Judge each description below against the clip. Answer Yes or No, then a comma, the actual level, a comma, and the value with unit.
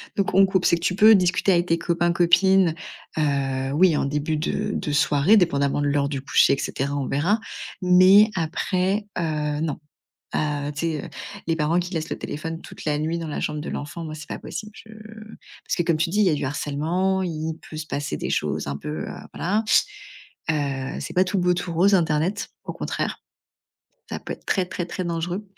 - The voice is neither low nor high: Yes, medium, 165 Hz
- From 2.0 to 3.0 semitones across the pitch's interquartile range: No, average, 3.6 semitones